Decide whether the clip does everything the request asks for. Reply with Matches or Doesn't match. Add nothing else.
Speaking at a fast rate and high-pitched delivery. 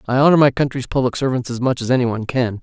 Doesn't match